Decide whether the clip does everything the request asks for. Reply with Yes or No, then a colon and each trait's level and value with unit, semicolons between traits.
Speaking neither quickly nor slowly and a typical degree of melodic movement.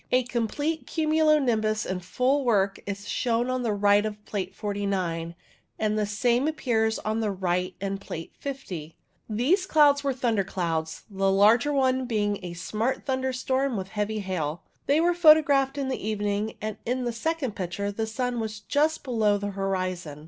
Yes: average, 170 wpm; average, 4.8 semitones